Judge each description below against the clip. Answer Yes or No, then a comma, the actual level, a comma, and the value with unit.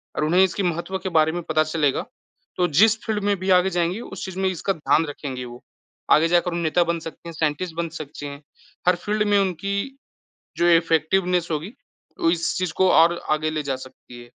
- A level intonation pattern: No, average, 3.2 semitones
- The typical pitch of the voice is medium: Yes, medium, 170 Hz